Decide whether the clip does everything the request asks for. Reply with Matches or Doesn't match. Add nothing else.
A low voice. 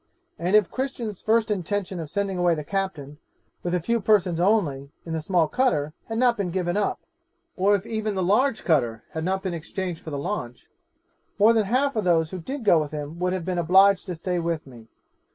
Doesn't match